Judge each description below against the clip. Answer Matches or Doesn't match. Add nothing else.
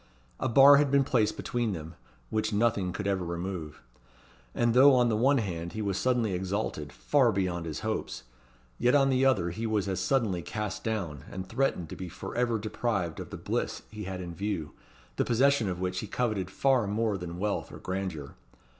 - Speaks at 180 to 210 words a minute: Matches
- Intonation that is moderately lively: Matches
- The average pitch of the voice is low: Matches